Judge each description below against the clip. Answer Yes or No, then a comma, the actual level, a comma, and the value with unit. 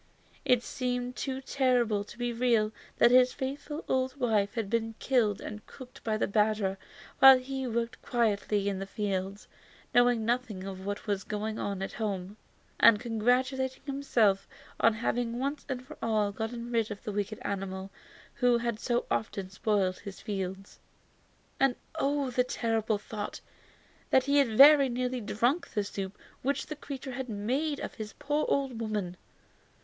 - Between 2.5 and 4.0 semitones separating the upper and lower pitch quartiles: Yes, average, 3.7 semitones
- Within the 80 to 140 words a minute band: No, average, 160 wpm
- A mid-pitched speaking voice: No, high, 230 Hz